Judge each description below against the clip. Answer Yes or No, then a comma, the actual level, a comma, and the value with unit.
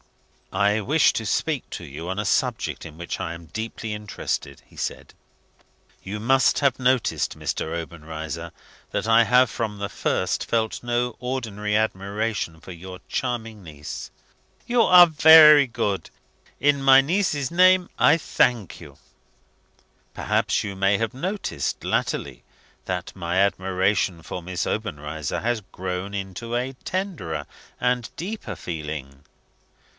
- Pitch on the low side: Yes, low, 105 Hz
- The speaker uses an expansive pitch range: Yes, wide, 6.2 semitones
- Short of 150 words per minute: Yes, slow, 135 wpm